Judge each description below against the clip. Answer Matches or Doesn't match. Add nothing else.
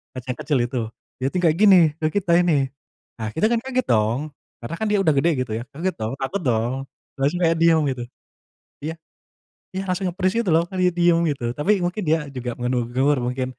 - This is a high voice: Doesn't match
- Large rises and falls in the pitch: Matches